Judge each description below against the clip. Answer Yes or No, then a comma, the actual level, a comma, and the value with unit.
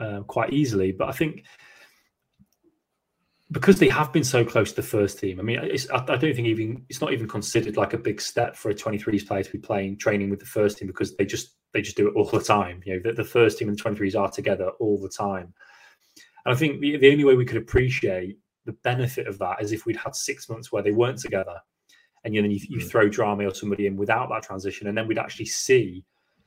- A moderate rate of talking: No, fast, 250 wpm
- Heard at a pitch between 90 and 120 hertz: Yes, low, 110 Hz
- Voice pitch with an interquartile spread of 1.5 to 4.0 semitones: No, average, 4.4 semitones